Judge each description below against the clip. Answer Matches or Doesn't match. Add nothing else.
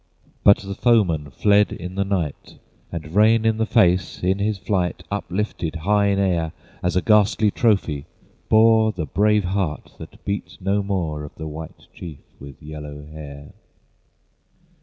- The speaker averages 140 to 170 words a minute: Matches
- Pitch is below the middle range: Matches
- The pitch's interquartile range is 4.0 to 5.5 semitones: Matches